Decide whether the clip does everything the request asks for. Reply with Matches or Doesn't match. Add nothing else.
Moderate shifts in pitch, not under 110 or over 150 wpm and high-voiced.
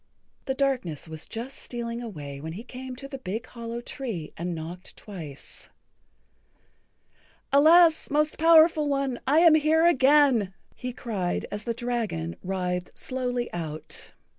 Doesn't match